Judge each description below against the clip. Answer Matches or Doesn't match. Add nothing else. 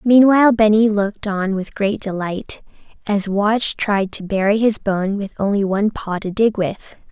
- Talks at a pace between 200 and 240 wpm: Doesn't match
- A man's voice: Doesn't match